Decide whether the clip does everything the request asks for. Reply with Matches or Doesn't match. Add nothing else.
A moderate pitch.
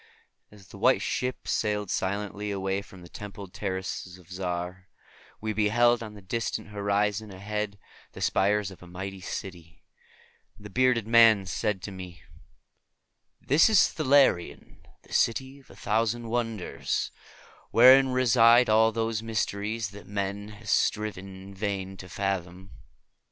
Doesn't match